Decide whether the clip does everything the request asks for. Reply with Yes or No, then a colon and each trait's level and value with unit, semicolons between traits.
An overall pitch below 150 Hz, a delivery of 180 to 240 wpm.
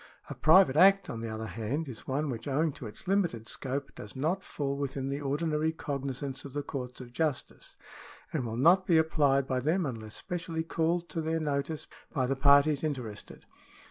Yes: medium, 140 Hz; average, 200 wpm